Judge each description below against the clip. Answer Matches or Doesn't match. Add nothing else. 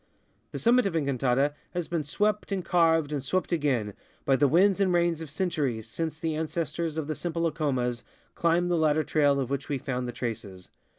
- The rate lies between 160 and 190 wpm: Doesn't match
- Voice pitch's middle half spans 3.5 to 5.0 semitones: Matches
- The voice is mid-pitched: Matches